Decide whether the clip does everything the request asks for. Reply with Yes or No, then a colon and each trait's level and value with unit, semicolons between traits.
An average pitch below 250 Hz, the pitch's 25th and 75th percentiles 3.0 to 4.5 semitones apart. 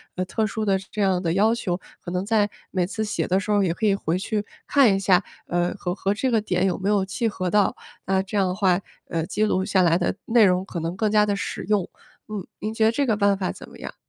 No: high, 195 Hz; narrow, 2.6 semitones